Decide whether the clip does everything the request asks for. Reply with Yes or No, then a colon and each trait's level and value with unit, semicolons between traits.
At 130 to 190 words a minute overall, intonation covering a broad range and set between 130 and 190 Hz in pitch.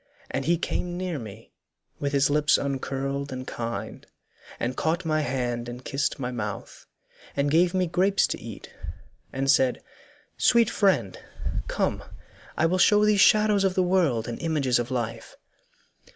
Yes: average, 155 wpm; wide, 6.1 semitones; medium, 140 Hz